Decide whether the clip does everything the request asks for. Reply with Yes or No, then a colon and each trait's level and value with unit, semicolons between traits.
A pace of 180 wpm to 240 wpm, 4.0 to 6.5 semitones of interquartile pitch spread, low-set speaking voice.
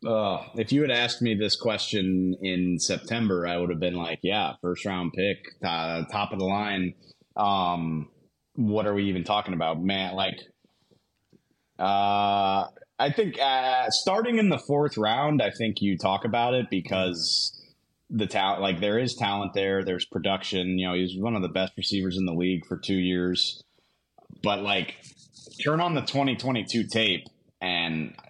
No: average, 170 wpm; average, 4.5 semitones; low, 100 Hz